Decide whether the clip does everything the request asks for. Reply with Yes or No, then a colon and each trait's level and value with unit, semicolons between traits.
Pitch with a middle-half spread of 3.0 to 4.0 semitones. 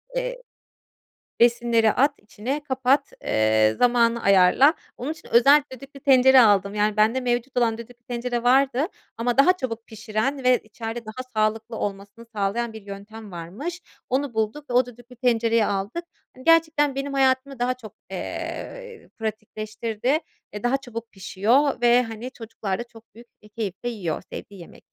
Yes: average, 3.4 semitones